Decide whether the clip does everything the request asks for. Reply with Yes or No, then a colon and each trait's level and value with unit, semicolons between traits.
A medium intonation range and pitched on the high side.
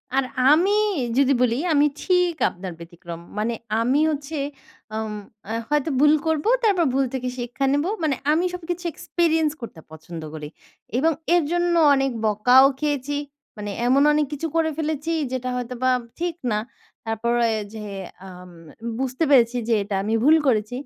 No: wide, 5.8 semitones; very high, 270 Hz